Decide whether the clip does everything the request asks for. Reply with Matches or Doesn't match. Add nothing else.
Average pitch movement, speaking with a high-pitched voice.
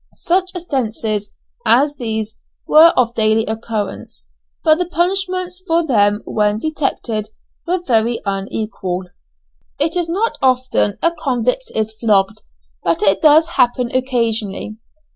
Doesn't match